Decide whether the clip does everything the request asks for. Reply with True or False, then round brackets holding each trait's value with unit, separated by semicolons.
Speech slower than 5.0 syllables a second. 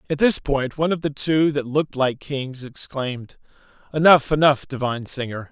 False (5.2 syllables/s)